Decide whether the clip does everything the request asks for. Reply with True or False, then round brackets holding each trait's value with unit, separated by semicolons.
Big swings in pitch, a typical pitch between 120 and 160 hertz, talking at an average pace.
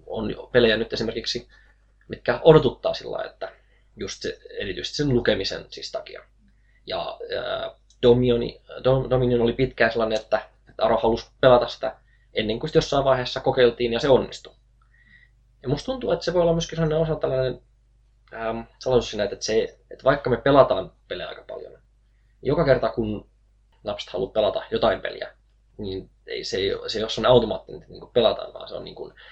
False (5.8 semitones; 125 Hz; 170 wpm)